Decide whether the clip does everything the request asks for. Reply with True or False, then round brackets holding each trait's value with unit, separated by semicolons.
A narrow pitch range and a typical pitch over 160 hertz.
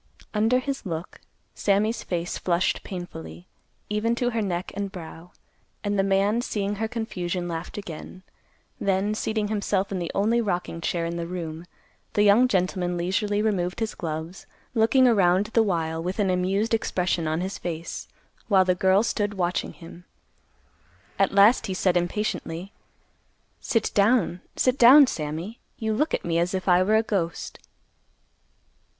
False (3.5 semitones; 190 Hz)